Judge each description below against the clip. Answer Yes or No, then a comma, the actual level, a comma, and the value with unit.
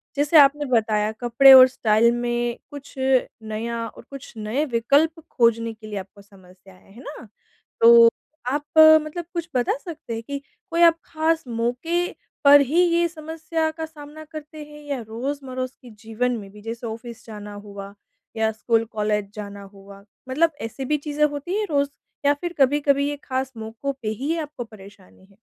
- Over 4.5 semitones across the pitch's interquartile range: Yes, average, 5.2 semitones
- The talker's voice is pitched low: No, very high, 255 Hz